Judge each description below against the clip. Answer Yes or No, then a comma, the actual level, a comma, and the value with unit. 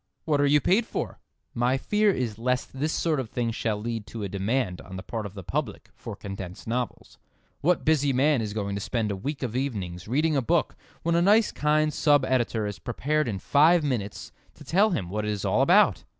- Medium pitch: No, low, 125 Hz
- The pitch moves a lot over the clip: Yes, wide, 6.2 semitones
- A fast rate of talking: Yes, fast, 220 wpm